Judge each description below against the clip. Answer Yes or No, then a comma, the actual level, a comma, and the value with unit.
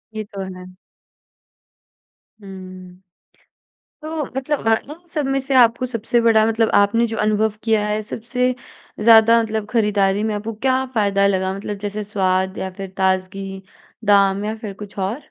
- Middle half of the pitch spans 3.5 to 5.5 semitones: No, average, 2.9 semitones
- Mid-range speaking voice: No, high, 210 Hz